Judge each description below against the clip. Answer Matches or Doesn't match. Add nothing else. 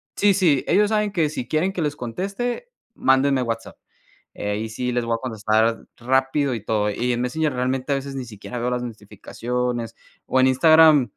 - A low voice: Matches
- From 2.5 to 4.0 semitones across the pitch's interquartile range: Doesn't match